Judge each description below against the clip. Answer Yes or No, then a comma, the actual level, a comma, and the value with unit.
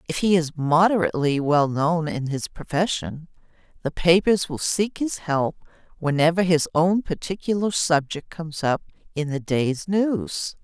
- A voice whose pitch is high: No, medium, 165 Hz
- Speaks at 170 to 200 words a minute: No, average, 140 wpm